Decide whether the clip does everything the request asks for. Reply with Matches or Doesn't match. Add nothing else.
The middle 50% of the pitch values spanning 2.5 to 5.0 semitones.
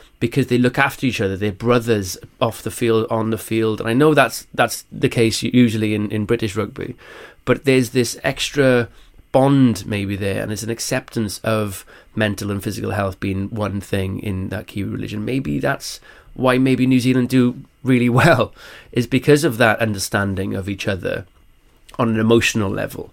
Matches